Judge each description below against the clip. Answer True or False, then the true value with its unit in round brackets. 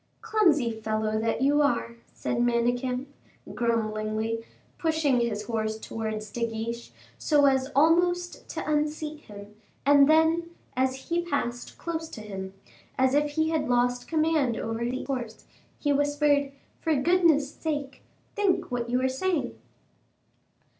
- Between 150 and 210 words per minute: False (135 wpm)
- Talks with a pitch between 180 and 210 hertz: False (265 Hz)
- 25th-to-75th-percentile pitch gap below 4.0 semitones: False (4.8 semitones)